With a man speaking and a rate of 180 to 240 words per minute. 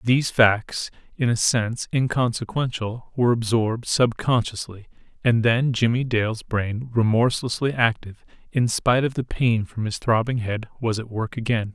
No: male; average, 150 wpm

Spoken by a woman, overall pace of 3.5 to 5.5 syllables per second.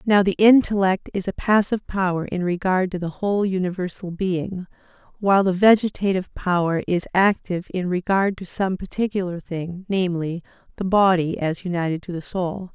Yes: female; 5.3 syllables/s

